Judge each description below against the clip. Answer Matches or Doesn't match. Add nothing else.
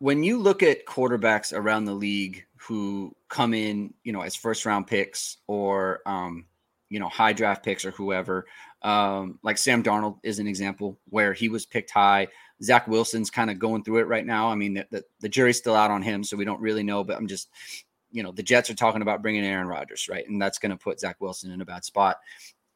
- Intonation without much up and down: Matches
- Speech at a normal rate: Doesn't match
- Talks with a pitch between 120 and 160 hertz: Doesn't match